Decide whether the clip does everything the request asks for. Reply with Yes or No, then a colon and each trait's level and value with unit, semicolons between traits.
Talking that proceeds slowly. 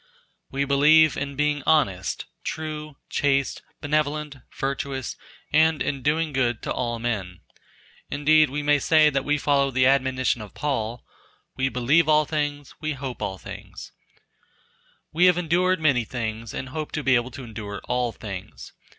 No: average, 155 wpm